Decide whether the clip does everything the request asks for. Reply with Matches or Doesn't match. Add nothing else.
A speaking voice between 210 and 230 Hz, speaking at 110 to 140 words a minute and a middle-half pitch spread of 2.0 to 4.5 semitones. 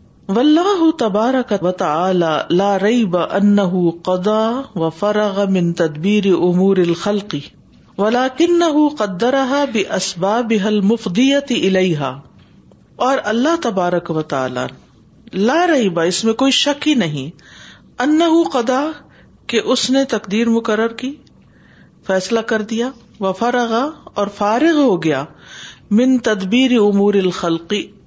Doesn't match